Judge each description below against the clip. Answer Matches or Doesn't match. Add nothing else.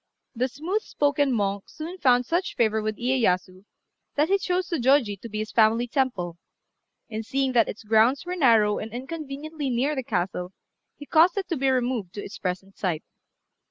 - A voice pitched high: Matches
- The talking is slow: Doesn't match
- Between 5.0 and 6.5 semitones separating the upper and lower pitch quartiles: Matches